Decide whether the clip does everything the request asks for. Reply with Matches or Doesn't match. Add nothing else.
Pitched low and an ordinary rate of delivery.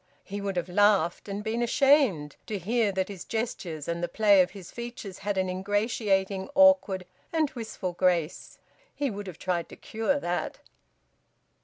Doesn't match